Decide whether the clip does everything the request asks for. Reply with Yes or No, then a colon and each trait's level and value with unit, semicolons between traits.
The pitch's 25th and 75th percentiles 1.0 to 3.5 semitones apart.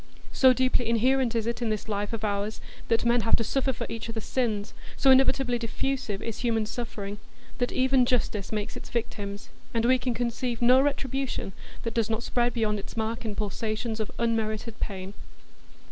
Yes: narrow, 2.4 semitones